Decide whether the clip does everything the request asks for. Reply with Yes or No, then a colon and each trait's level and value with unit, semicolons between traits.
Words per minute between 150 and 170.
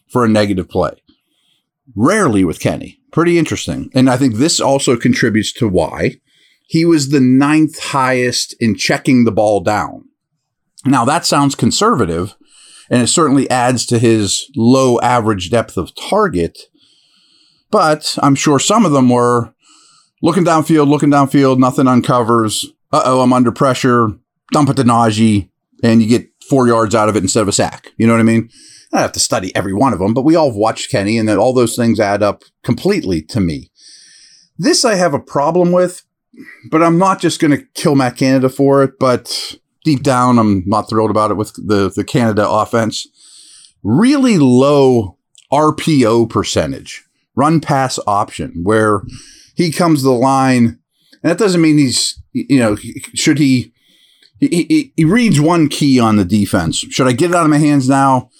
No: average, 180 wpm